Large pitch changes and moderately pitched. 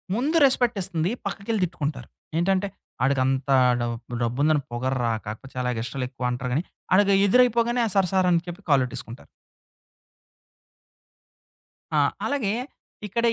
Yes: wide, 7.9 semitones; medium, 160 Hz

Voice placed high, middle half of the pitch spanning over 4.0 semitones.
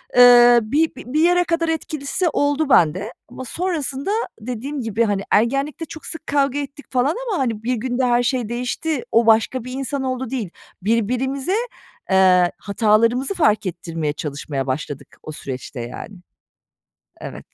Yes: high, 245 Hz; average, 5.0 semitones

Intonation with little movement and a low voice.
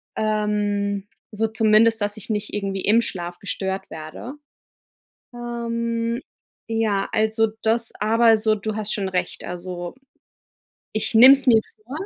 No: narrow, 2.2 semitones; high, 215 Hz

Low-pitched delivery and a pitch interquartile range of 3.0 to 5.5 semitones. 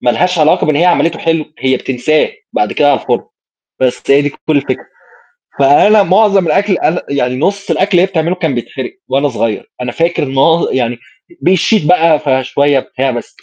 No: medium, 150 Hz; average, 5.0 semitones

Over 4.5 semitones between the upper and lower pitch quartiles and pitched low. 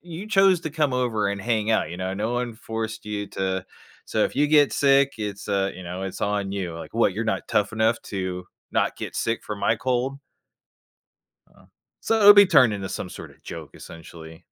Yes: average, 5.2 semitones; low, 110 Hz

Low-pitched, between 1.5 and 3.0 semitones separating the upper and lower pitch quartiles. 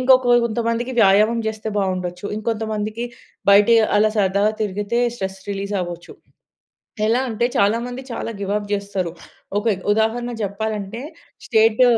No: high, 215 Hz; narrow, 2.5 semitones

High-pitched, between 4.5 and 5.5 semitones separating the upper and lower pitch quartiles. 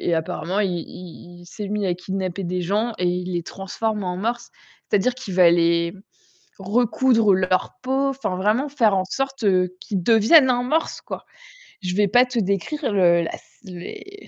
Yes: high, 200 Hz; average, 5.0 semitones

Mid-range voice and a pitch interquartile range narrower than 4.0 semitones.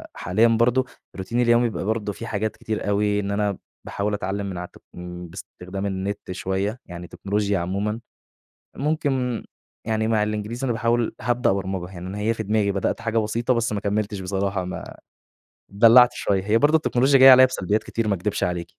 No: low, 105 Hz; average, 3.2 semitones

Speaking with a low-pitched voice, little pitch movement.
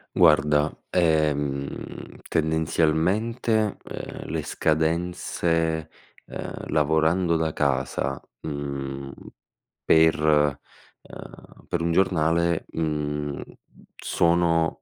Yes: very low, 80 Hz; narrow, 2.1 semitones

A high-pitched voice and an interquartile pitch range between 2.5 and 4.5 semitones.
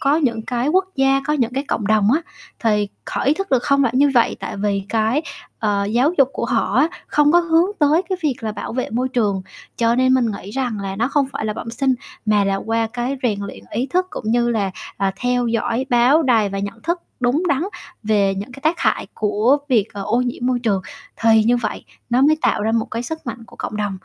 Yes: high, 240 Hz; average, 4.1 semitones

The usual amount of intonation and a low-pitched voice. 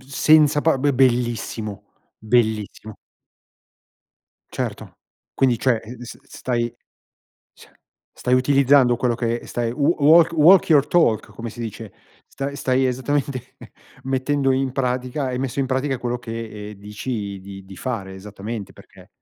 Yes: average, 3.4 semitones; low, 125 Hz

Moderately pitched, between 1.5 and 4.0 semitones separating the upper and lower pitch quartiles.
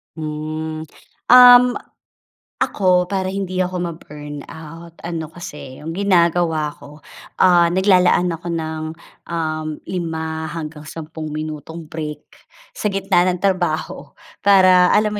Yes: medium, 165 Hz; average, 2.8 semitones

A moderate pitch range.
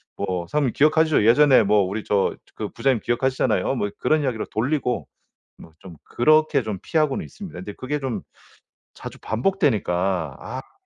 No: wide, 6.3 semitones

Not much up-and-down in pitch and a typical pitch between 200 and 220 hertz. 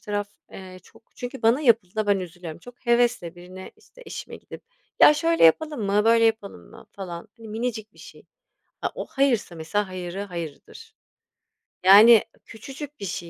No: average, 4.6 semitones; high, 210 Hz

